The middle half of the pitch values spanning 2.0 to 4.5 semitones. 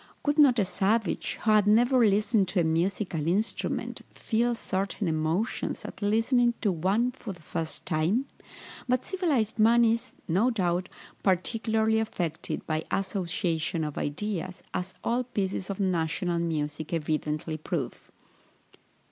No: average, 5.1 semitones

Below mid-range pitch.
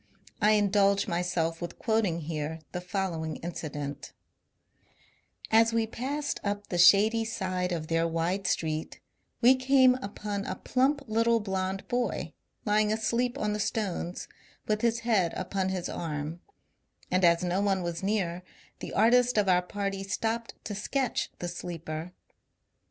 No: high, 195 Hz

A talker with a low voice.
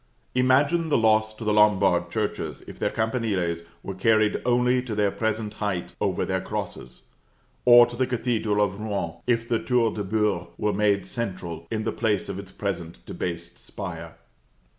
Yes: low, 105 Hz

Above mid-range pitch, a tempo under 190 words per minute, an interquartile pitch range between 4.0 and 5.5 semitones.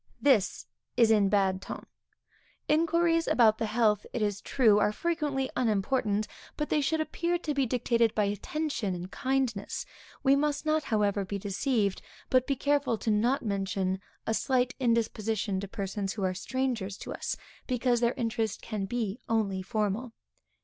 Yes: high, 225 Hz; average, 160 wpm; average, 4.7 semitones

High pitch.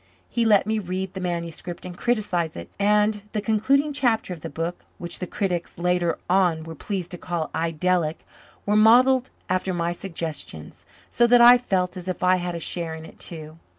No: medium, 180 Hz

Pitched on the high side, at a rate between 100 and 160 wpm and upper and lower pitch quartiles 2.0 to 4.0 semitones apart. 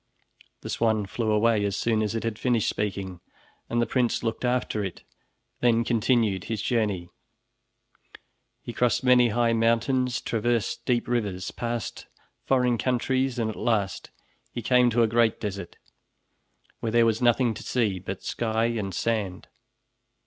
No: low, 115 Hz; average, 155 wpm; narrow, 2.4 semitones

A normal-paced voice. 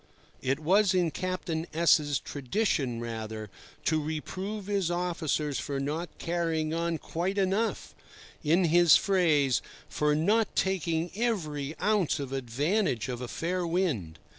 No: slow, 125 wpm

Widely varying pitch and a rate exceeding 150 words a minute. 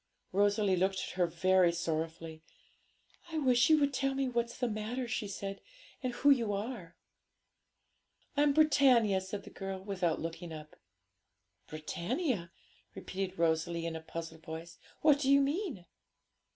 No: wide, 7.2 semitones; average, 145 wpm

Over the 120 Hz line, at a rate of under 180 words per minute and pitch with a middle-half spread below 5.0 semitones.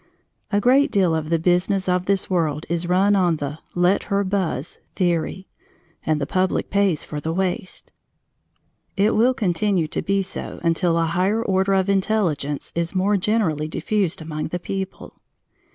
Yes: medium, 185 Hz; average, 165 wpm; average, 3.2 semitones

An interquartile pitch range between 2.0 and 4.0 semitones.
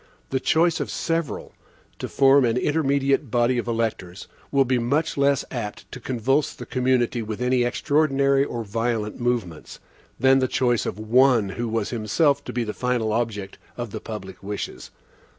Yes: average, 3.4 semitones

